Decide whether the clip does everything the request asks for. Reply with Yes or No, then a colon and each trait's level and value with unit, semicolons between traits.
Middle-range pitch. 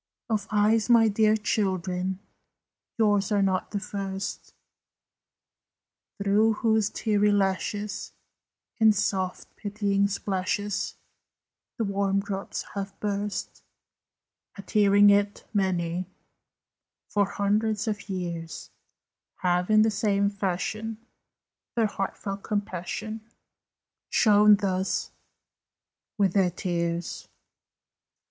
No: high, 200 Hz